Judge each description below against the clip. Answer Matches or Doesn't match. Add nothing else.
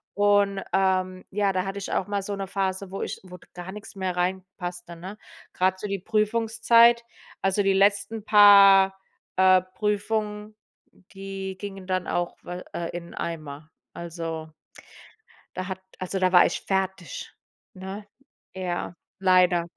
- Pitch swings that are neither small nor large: Doesn't match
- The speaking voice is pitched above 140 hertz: Matches